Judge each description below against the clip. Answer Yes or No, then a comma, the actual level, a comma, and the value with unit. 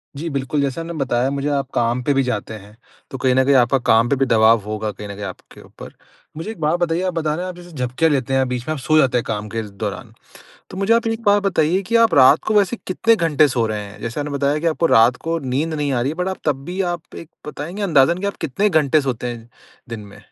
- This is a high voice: No, medium, 140 Hz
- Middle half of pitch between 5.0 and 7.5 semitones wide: Yes, wide, 5.6 semitones